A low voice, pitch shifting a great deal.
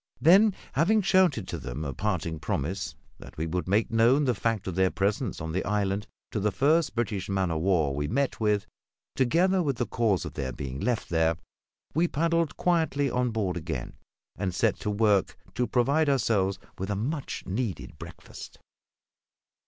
Yes: low, 105 Hz; wide, 7.1 semitones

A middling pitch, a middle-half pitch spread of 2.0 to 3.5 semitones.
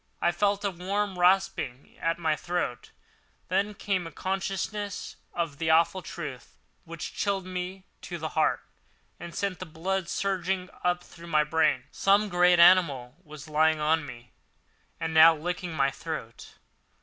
Yes: medium, 175 Hz; average, 3.1 semitones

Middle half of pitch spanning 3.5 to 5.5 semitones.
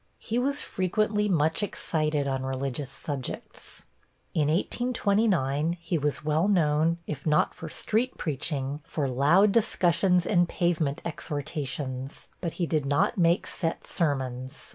Yes: average, 4.3 semitones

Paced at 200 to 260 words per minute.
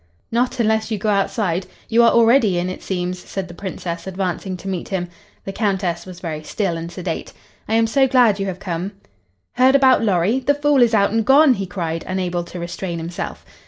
Yes: fast, 205 wpm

